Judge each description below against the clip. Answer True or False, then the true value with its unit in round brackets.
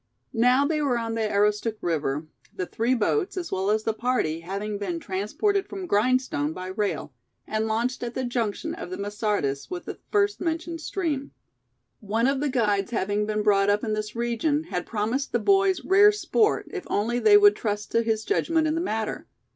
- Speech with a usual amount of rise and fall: False (7.1 semitones)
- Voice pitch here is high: True (230 Hz)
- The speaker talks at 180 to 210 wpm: True (195 wpm)